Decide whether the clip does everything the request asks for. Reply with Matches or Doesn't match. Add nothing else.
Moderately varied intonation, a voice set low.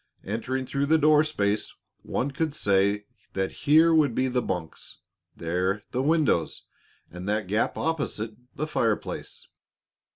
Doesn't match